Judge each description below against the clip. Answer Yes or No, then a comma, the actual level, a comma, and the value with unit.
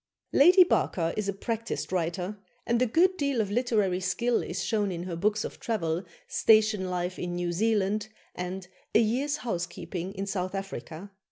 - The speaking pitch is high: Yes, high, 200 Hz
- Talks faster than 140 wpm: Yes, average, 175 wpm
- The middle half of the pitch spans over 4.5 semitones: No, average, 4.1 semitones